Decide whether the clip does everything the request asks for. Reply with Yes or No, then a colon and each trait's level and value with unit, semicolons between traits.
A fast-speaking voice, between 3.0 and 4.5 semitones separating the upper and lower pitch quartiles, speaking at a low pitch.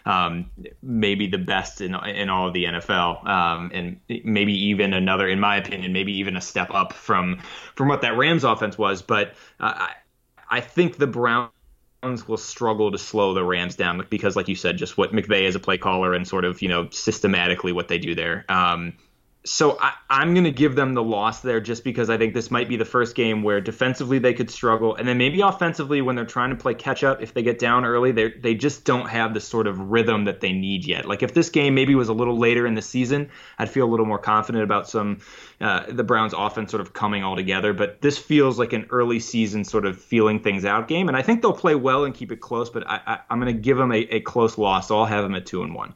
Yes: fast, 245 wpm; average, 3.7 semitones; low, 110 Hz